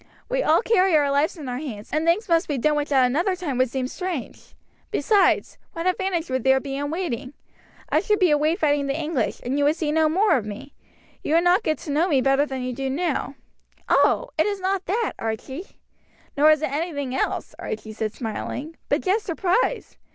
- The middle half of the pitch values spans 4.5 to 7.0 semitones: Yes, average, 4.9 semitones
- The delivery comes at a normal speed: No, fast, 215 wpm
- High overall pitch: Yes, very high, 300 Hz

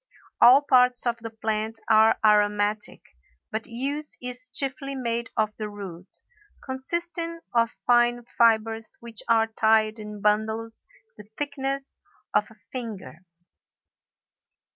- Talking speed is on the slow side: Yes, slow, 120 wpm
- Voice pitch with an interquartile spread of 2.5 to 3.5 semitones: Yes, average, 2.8 semitones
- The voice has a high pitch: Yes, high, 230 Hz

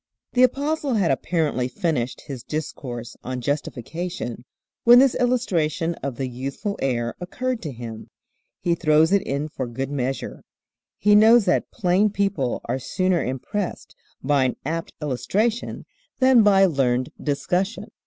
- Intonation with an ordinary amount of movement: No, wide, 7.8 semitones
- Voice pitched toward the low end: No, medium, 160 Hz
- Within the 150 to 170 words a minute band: No, average, 140 wpm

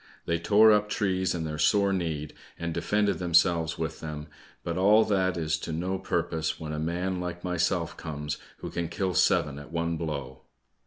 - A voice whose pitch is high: No, very low, 85 Hz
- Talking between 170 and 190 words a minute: Yes, average, 180 wpm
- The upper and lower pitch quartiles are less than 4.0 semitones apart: Yes, average, 2.8 semitones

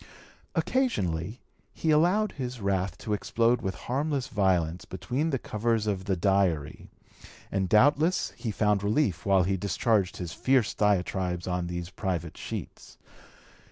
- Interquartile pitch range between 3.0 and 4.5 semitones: No, wide, 5.5 semitones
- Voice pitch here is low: Yes, low, 100 Hz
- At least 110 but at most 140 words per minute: Yes, slow, 135 wpm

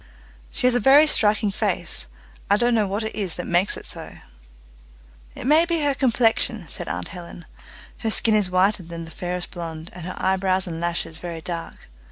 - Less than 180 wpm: No, average, 195 wpm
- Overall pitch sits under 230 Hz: Yes, high, 190 Hz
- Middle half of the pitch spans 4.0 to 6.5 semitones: Yes, average, 4.6 semitones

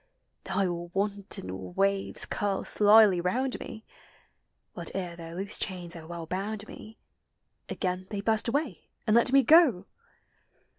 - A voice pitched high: Yes, high, 195 Hz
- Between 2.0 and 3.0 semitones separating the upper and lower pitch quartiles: No, average, 3.4 semitones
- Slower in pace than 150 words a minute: Yes, slow, 135 wpm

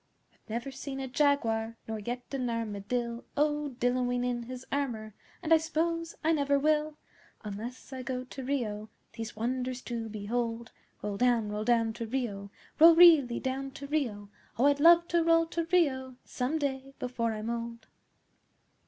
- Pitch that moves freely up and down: No, average, 3.7 semitones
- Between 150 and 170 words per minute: Yes, average, 165 wpm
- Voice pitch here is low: No, very high, 250 Hz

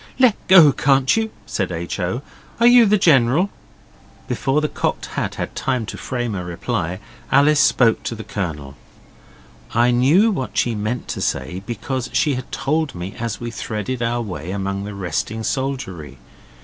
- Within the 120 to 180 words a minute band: Yes, average, 170 wpm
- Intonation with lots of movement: Yes, wide, 6.1 semitones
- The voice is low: Yes, low, 120 Hz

